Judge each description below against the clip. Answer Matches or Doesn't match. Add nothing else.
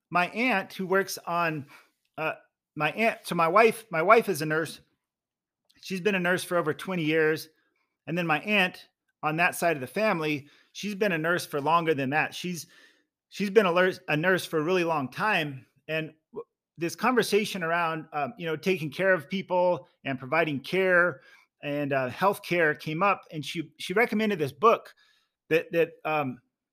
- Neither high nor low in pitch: Matches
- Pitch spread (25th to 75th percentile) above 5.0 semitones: Doesn't match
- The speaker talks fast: Doesn't match